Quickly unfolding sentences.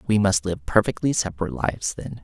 No: average, 190 wpm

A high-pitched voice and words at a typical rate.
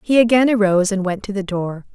No: high, 205 Hz; fast, 245 wpm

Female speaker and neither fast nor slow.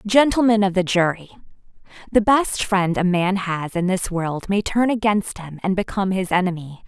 Yes: female; average, 185 wpm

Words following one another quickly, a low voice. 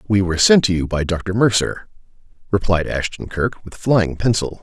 No: average, 180 wpm; very low, 95 Hz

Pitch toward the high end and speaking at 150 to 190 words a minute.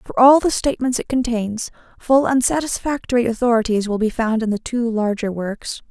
Yes: high, 235 Hz; average, 185 wpm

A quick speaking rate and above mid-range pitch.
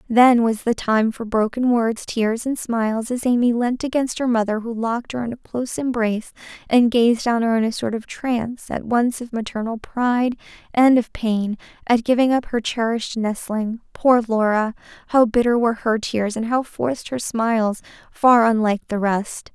No: average, 185 wpm; high, 230 Hz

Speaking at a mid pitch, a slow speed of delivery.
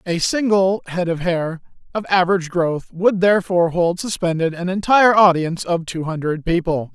No: medium, 180 Hz; average, 165 wpm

